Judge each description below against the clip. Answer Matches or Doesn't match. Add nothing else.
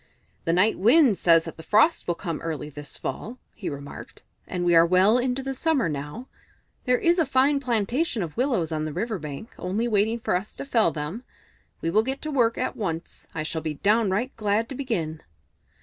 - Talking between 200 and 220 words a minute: Matches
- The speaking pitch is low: Doesn't match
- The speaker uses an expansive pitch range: Matches